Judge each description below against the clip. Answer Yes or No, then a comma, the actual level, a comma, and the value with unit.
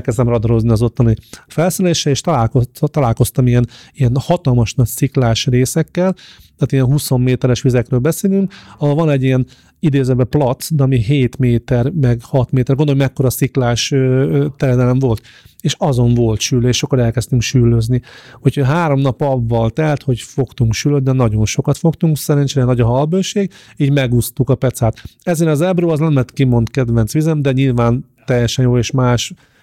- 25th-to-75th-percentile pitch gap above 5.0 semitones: No, average, 2.9 semitones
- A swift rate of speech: Yes, fast, 160 wpm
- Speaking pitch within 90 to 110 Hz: No, low, 130 Hz